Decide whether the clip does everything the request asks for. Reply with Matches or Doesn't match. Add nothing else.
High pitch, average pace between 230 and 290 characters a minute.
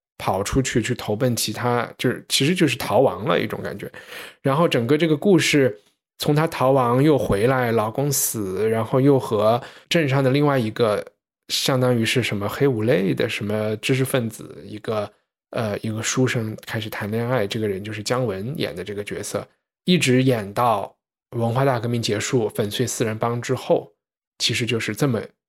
Doesn't match